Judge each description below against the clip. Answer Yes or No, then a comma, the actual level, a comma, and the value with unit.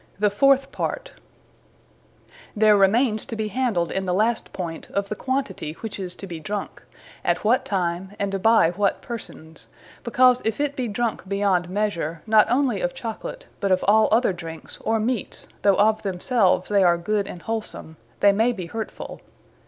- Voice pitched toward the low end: No, high, 205 Hz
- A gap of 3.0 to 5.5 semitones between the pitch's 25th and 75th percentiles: Yes, average, 3.6 semitones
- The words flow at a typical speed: Yes, average, 175 wpm